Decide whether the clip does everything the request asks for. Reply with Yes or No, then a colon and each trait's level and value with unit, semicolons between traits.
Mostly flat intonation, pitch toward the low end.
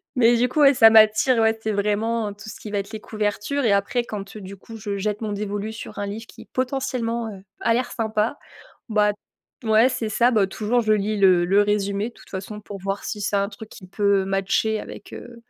No: narrow, 2.2 semitones; high, 215 Hz